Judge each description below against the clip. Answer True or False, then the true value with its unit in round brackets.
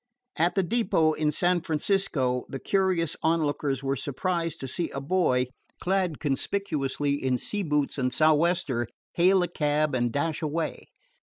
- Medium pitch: True (155 Hz)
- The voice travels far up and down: False (4.2 semitones)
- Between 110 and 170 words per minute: True (150 wpm)